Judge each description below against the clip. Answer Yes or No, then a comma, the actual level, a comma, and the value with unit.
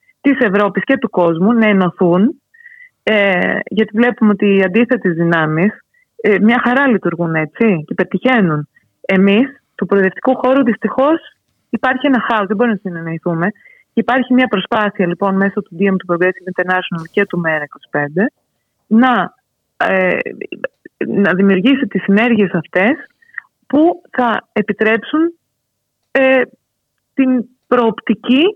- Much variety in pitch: No, average, 5.0 semitones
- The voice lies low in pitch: No, high, 215 Hz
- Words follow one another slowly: No, average, 125 wpm